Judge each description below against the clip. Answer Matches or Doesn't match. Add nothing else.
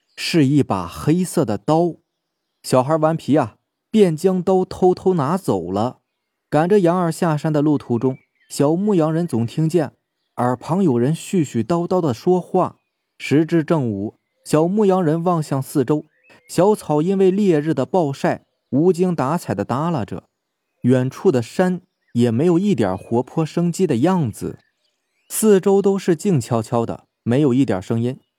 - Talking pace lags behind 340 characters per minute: Matches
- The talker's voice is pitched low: Doesn't match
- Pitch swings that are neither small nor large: Doesn't match